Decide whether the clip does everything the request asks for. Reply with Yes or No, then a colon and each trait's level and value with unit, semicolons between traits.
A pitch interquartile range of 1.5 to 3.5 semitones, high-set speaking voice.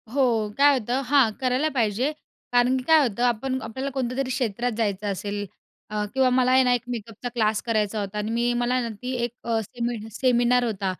Yes: average, 2.8 semitones; high, 240 Hz